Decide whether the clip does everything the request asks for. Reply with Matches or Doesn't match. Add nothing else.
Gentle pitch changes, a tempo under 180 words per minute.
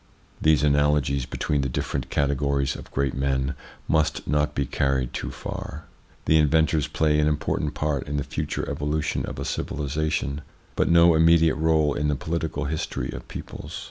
Matches